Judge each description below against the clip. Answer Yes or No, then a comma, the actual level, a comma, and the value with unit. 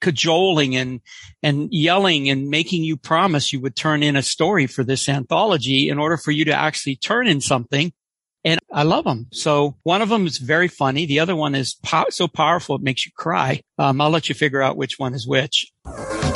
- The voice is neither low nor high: Yes, medium, 150 Hz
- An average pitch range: Yes, average, 3.0 semitones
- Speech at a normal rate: No, fast, 215 wpm